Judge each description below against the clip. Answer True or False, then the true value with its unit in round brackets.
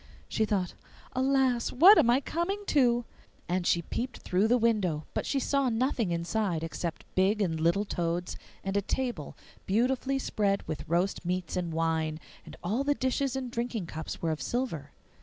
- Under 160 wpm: False (170 wpm)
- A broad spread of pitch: True (6.8 semitones)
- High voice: True (210 Hz)